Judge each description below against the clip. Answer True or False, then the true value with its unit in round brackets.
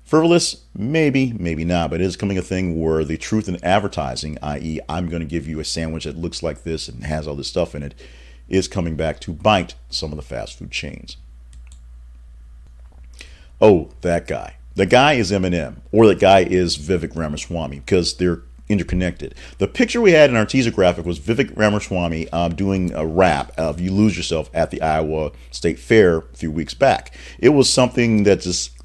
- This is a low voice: True (85 Hz)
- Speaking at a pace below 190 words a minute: False (195 wpm)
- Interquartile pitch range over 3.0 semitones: True (4.8 semitones)